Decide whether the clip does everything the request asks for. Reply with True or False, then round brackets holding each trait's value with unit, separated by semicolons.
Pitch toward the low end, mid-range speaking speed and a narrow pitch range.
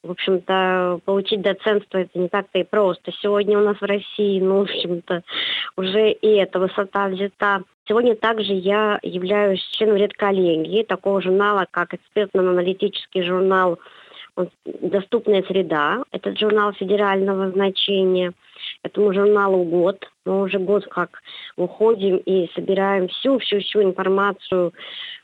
False (195 Hz; 120 wpm; 1.8 semitones)